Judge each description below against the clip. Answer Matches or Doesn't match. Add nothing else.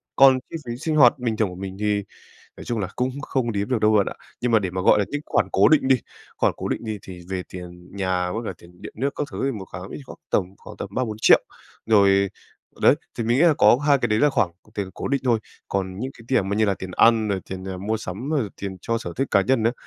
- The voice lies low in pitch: Matches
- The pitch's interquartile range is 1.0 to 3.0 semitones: Doesn't match